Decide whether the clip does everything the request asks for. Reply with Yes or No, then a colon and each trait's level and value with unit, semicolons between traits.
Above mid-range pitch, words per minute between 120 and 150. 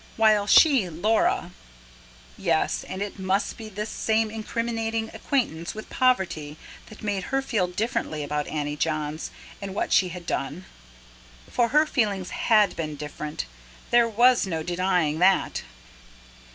Yes: high, 195 Hz; average, 140 wpm